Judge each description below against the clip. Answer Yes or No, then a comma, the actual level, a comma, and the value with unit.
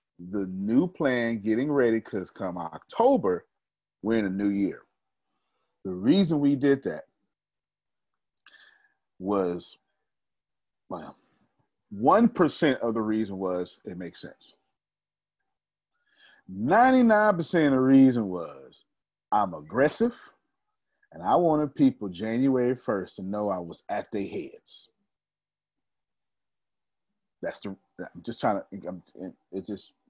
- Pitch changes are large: Yes, wide, 8.5 semitones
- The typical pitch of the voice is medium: No, low, 125 Hz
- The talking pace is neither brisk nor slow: No, slow, 115 wpm